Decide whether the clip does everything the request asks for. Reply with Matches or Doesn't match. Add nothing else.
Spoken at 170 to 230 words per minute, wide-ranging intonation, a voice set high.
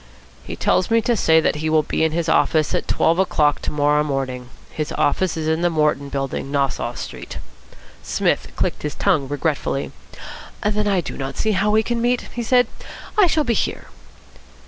Doesn't match